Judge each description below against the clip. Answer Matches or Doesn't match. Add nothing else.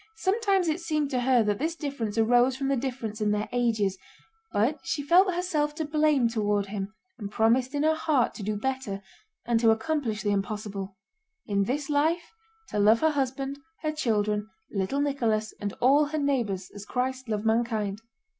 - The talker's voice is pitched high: Matches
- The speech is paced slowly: Doesn't match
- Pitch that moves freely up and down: Matches